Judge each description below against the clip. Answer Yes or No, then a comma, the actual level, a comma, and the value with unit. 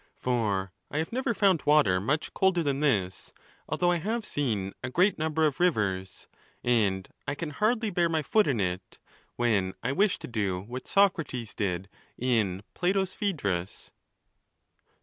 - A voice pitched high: No, low, 135 Hz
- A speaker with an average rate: Yes, average, 155 wpm